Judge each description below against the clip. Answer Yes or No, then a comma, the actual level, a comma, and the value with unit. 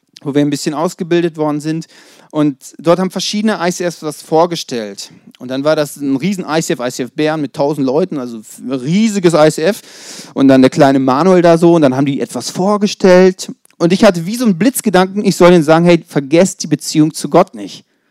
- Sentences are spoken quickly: Yes, fast, 200 wpm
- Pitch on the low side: No, medium, 165 Hz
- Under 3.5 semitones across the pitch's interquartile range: No, average, 4.1 semitones